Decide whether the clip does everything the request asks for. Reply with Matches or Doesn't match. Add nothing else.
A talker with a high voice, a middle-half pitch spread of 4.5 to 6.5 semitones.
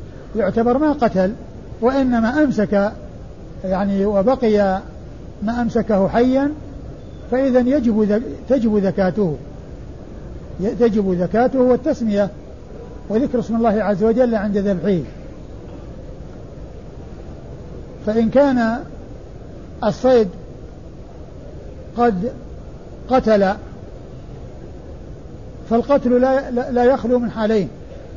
Doesn't match